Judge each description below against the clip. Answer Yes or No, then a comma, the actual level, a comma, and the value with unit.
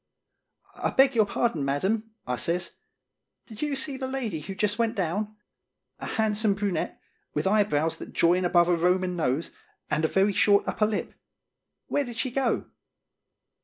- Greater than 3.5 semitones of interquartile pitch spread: Yes, average, 4.5 semitones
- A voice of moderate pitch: No, high, 205 Hz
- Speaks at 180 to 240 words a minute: No, average, 165 wpm